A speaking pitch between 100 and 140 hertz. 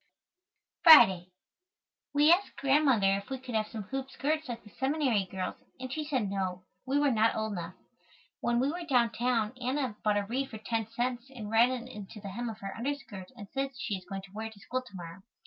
No: high, 235 Hz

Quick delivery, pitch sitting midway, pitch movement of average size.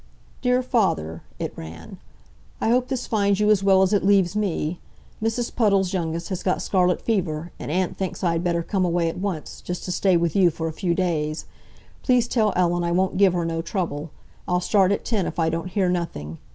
Yes: fast, 210 wpm; medium, 180 Hz; average, 3.2 semitones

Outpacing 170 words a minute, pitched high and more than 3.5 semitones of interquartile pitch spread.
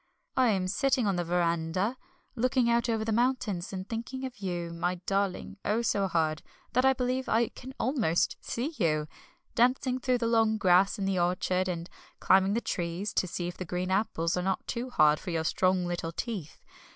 Yes: average, 195 wpm; high, 195 Hz; average, 5.1 semitones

